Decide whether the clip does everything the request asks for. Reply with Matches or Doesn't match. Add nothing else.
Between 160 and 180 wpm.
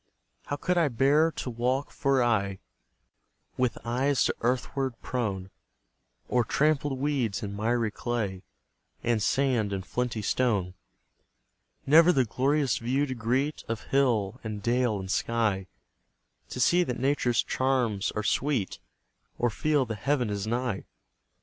Doesn't match